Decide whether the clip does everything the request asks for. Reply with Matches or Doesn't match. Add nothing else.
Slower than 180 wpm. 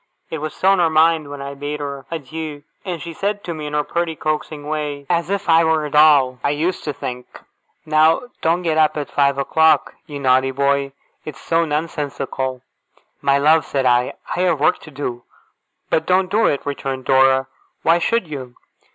Doesn't match